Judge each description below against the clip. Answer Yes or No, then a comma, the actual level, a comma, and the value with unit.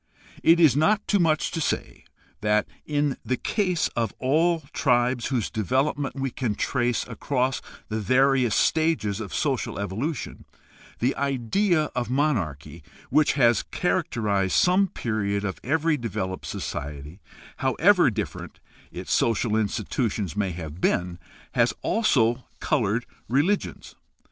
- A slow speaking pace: Yes, slow, 125 wpm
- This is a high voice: No, low, 125 Hz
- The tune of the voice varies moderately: No, wide, 6.1 semitones